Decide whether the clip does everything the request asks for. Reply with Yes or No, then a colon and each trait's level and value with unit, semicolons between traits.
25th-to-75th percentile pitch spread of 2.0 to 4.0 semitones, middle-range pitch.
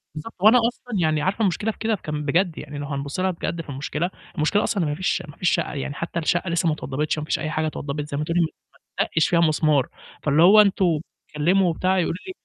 Yes: average, 3.7 semitones; medium, 165 Hz